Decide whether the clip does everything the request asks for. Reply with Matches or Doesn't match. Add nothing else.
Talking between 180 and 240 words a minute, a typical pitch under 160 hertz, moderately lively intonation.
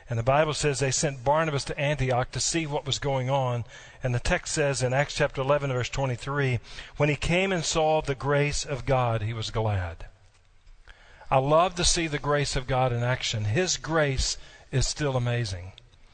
Matches